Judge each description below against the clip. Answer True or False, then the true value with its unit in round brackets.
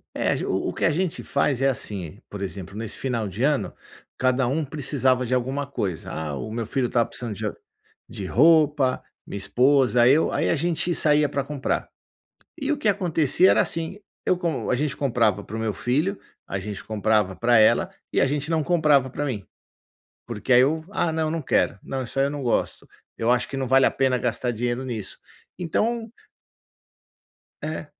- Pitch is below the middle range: True (130 Hz)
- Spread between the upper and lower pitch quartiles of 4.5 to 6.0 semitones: True (4.8 semitones)